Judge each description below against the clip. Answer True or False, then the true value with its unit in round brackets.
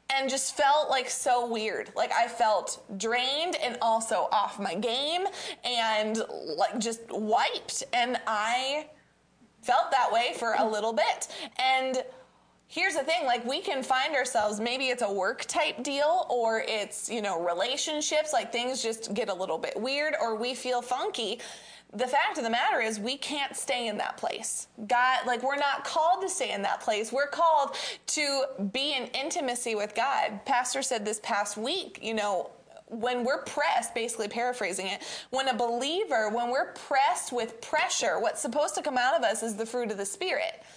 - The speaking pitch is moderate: False (250 Hz)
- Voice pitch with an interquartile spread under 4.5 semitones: True (4.0 semitones)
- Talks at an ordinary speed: True (185 wpm)